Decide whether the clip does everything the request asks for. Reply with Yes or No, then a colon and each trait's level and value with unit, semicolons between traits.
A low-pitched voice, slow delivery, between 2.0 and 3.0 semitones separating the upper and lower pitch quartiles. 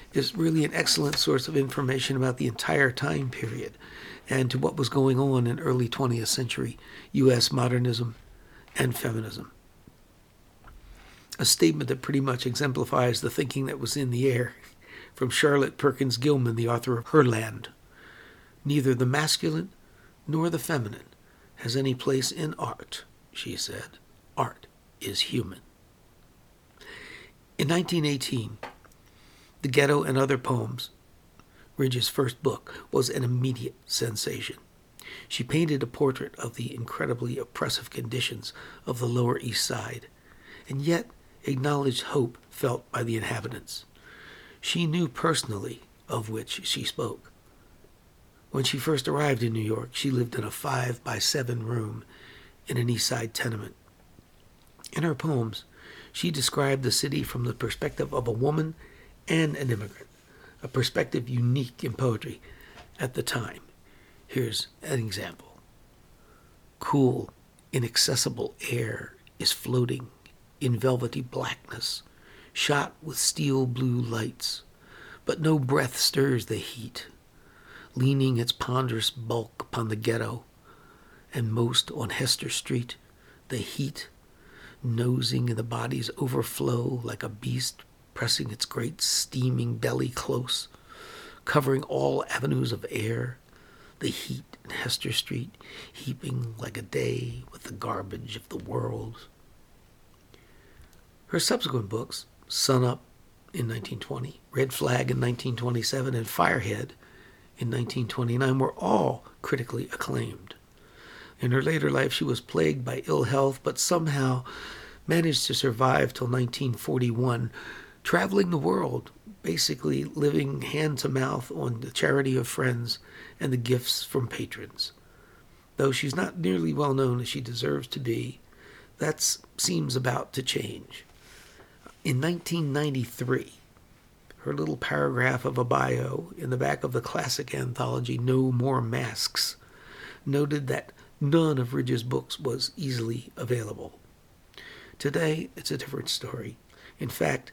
Yes: low, 125 Hz; slow, 130 wpm; average, 2.7 semitones